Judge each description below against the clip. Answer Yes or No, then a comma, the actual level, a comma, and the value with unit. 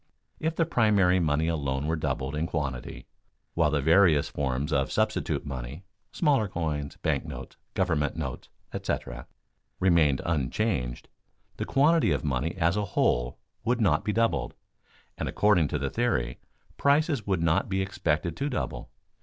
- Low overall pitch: Yes, very low, 80 Hz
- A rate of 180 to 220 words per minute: No, average, 150 wpm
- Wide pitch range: Yes, wide, 6.3 semitones